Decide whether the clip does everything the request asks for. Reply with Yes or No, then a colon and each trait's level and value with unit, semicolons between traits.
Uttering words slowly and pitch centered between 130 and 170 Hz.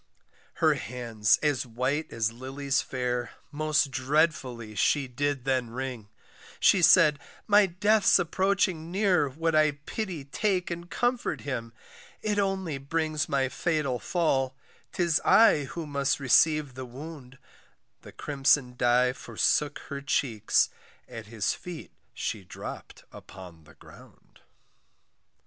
Yes: slow, 125 wpm; medium, 140 Hz